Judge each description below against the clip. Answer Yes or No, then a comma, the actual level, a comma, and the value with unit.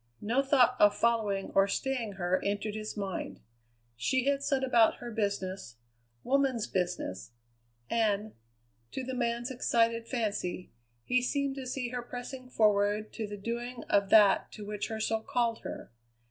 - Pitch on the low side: No, high, 225 Hz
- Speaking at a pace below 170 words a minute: Yes, average, 155 wpm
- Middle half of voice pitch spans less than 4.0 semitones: Yes, average, 3.6 semitones